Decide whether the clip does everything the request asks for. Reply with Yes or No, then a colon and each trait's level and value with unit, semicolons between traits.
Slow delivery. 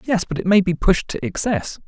No: fast, 255 wpm